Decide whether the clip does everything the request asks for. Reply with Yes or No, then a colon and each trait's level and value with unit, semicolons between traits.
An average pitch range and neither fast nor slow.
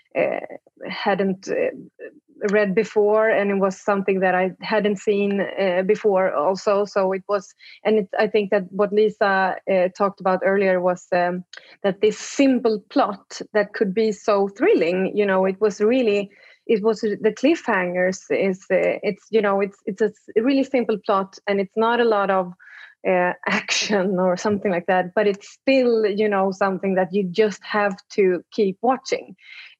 No: narrow, 2.3 semitones; average, 175 wpm